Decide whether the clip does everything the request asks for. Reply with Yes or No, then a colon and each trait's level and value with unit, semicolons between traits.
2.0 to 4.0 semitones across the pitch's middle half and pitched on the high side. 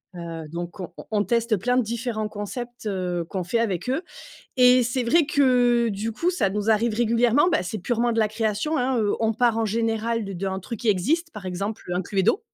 Yes: average, 3.5 semitones; high, 225 Hz